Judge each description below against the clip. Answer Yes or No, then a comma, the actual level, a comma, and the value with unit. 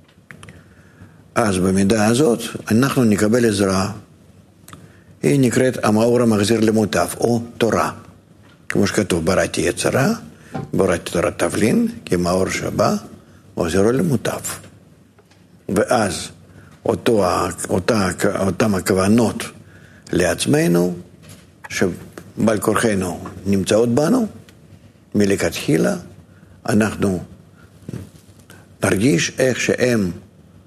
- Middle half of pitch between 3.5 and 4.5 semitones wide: Yes, average, 3.9 semitones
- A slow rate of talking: Yes, slow, 75 wpm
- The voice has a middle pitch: No, low, 105 Hz